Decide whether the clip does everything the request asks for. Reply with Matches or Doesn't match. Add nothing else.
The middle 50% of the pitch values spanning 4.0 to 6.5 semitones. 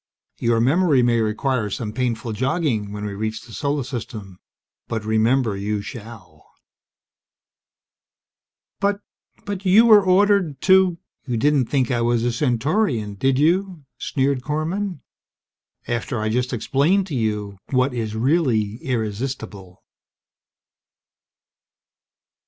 Matches